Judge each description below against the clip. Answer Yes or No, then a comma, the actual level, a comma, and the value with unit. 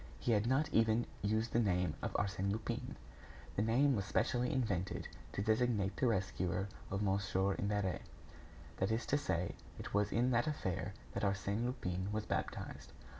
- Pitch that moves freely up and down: No, average, 3.3 semitones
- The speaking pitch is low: Yes, low, 105 Hz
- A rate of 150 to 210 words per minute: Yes, average, 165 wpm